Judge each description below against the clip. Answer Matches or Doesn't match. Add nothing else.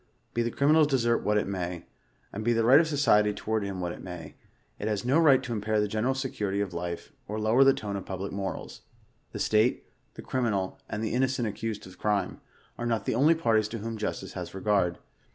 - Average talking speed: Doesn't match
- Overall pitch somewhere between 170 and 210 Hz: Doesn't match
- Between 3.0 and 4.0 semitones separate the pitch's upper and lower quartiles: Matches